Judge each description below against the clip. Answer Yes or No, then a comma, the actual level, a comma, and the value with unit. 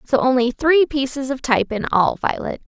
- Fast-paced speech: No, average, 195 wpm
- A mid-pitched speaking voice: No, very high, 265 Hz